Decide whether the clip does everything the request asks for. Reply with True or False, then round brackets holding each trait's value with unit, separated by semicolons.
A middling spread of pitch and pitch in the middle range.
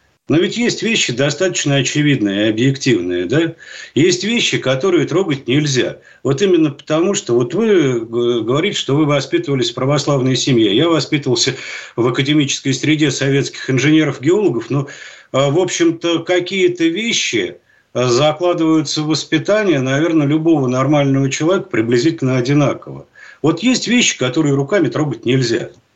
True (4.4 semitones; 150 Hz)